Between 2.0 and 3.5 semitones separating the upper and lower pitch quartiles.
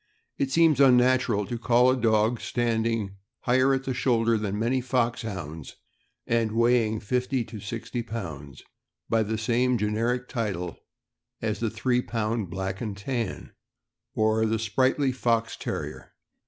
Yes: narrow, 2.6 semitones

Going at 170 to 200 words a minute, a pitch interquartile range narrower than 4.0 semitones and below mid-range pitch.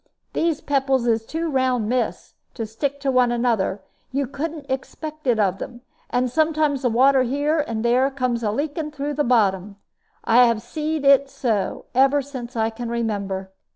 No: average, 180 wpm; average, 3.6 semitones; very high, 255 Hz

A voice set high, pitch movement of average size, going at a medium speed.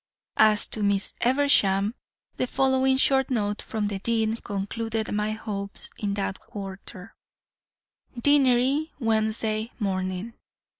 No: high, 220 Hz; average, 3.6 semitones; slow, 110 wpm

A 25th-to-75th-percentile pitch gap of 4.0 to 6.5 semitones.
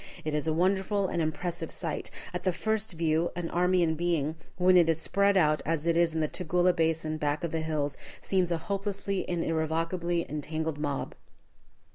No: narrow, 2.4 semitones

